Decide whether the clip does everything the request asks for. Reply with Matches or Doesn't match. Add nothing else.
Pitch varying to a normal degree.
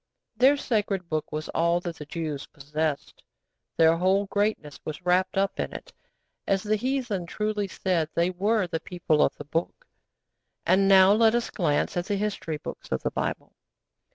Matches